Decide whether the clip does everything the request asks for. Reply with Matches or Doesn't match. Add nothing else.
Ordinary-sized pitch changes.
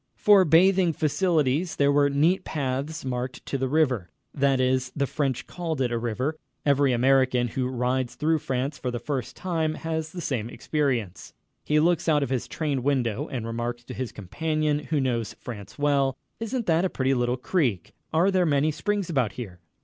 Matches